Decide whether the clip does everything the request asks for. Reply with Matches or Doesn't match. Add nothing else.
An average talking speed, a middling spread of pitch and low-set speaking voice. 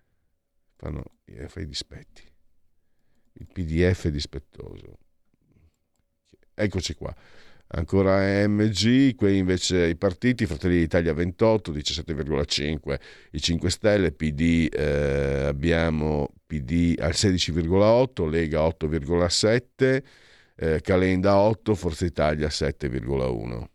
Doesn't match